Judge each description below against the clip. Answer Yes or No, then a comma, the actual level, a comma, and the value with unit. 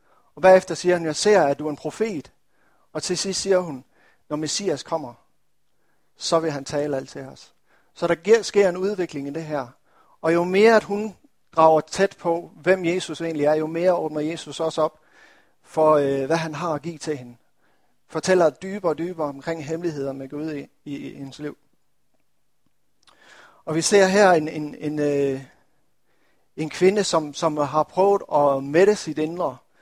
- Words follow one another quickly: No, average, 185 wpm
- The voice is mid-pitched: Yes, medium, 160 Hz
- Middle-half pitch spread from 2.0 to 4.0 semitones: Yes, average, 3.3 semitones